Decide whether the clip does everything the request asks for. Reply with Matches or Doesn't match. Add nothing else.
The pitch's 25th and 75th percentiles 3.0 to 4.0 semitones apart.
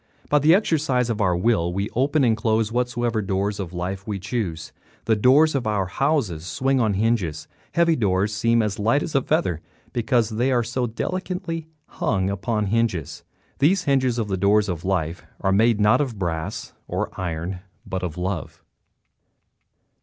Doesn't match